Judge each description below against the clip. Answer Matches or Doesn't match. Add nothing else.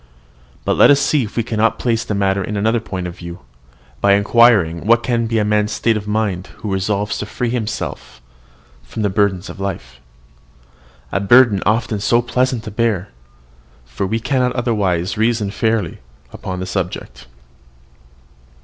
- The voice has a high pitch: Doesn't match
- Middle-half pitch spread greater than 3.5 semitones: Doesn't match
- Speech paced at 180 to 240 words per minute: Doesn't match